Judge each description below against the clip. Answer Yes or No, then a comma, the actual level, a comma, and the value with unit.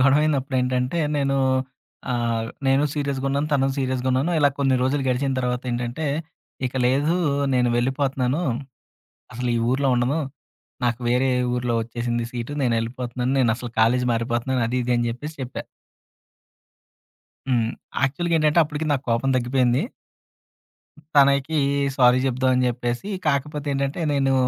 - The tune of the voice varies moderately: No, narrow, 2.3 semitones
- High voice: No, low, 130 Hz